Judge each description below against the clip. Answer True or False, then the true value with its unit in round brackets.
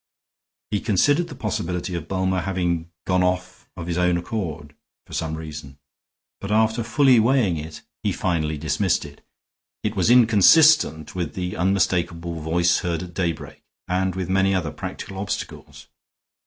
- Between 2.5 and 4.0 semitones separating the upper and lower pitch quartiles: True (3.0 semitones)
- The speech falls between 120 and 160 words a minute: True (150 wpm)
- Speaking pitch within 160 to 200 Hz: False (90 Hz)